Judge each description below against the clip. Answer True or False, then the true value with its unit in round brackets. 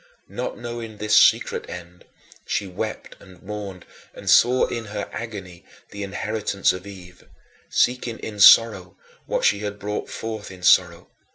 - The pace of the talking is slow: False (150 wpm)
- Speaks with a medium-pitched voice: False (100 Hz)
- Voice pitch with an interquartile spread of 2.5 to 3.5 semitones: True (3.1 semitones)